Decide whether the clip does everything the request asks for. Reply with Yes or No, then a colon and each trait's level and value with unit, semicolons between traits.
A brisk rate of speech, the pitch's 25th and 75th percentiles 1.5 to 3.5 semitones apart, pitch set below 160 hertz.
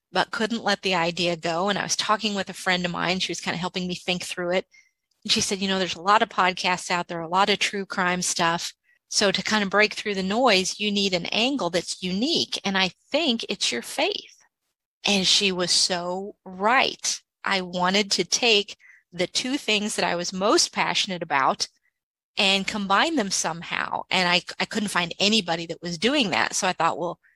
No: fast, 215 wpm; average, 2.8 semitones; high, 190 Hz